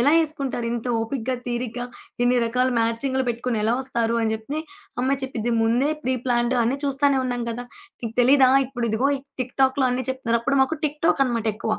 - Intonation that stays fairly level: Yes, narrow, 2.3 semitones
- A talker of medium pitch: No, very high, 250 Hz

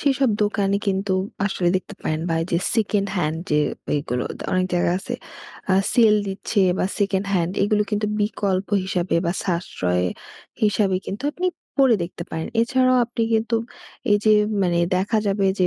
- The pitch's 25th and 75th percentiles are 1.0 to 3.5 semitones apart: Yes, average, 3.2 semitones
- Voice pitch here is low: No, high, 195 Hz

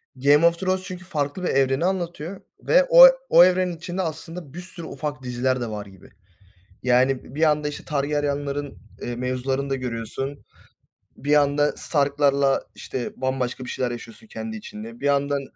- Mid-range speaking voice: Yes, medium, 145 Hz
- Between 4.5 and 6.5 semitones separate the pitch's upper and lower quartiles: Yes, average, 4.8 semitones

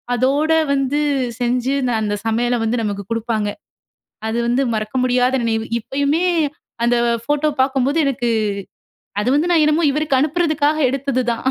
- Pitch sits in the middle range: No, very high, 260 Hz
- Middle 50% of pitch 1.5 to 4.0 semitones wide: Yes, average, 3.7 semitones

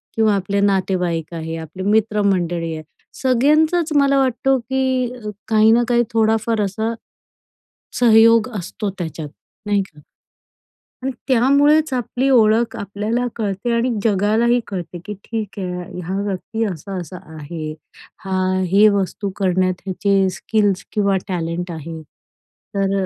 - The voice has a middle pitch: No, high, 205 Hz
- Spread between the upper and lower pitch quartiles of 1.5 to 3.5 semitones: No, average, 4.0 semitones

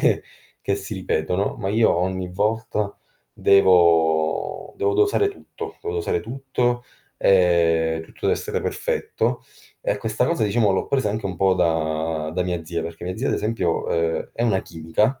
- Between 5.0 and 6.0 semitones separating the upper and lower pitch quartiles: Yes, average, 5.3 semitones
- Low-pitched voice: Yes, very low, 95 Hz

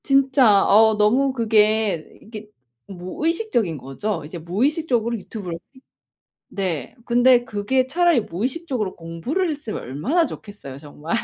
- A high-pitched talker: Yes, high, 220 Hz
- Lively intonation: Yes, wide, 6.2 semitones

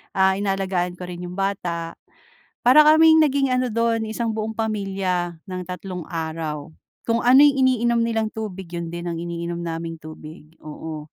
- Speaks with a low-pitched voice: No, high, 190 Hz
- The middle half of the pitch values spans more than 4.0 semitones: Yes, average, 5.2 semitones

